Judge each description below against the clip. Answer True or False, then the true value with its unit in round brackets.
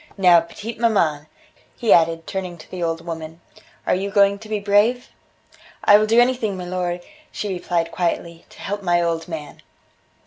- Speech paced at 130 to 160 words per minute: False (170 wpm)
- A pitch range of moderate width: True (3.5 semitones)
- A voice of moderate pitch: True (180 Hz)